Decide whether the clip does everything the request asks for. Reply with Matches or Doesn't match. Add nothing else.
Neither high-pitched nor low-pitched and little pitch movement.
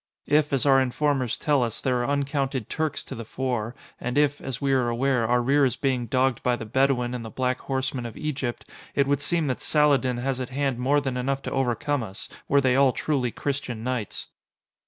Doesn't match